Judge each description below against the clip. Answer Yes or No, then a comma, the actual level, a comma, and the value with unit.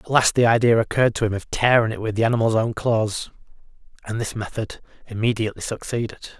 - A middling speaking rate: Yes, average, 190 wpm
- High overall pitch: No, low, 110 Hz